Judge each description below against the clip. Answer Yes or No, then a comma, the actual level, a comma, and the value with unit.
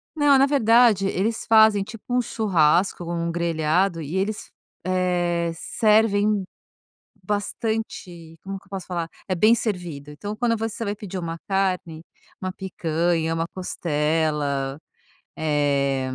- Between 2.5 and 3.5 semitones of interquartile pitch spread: No, average, 4.3 semitones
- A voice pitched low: No, medium, 185 Hz